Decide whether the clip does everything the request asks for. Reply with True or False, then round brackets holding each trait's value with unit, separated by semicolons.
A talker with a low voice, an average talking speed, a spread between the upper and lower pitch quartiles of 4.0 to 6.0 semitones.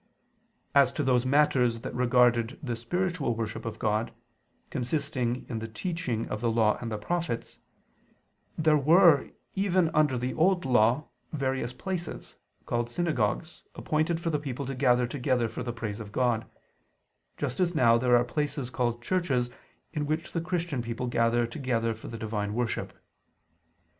True (125 Hz; 160 wpm; 4.6 semitones)